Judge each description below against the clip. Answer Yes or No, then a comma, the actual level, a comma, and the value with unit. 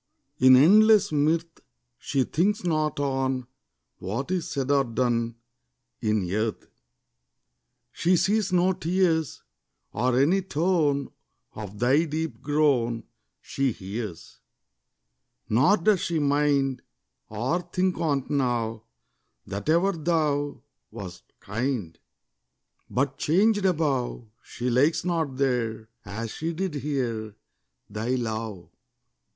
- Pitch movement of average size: No, wide, 6.0 semitones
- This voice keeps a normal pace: No, slow, 105 wpm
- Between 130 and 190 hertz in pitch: Yes, medium, 140 Hz